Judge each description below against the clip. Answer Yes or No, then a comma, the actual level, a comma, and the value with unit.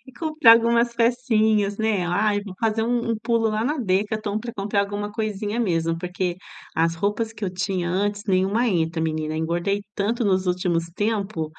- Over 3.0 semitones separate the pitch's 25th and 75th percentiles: Yes, average, 3.6 semitones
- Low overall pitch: No, high, 205 Hz